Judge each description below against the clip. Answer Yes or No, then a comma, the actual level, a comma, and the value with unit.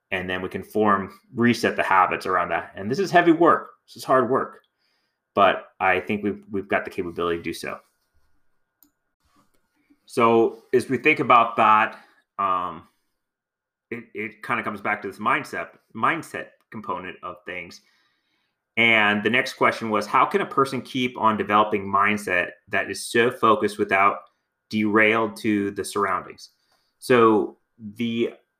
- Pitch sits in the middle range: No, low, 110 Hz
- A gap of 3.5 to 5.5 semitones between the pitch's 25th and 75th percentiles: Yes, average, 4.1 semitones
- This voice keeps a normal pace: Yes, average, 155 wpm